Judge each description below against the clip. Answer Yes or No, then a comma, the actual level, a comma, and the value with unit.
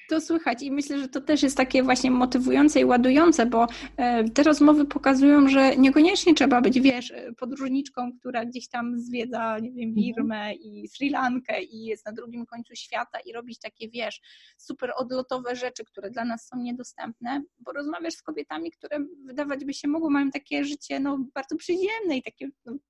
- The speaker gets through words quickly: Yes, fast, 180 wpm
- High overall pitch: Yes, very high, 260 Hz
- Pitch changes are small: No, average, 3.3 semitones